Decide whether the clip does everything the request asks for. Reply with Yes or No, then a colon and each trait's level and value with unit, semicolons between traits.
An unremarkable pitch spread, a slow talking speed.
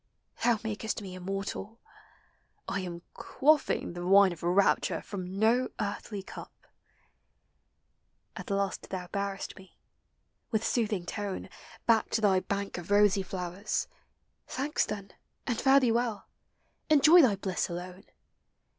Yes: average, 3.1 semitones; slow, 130 wpm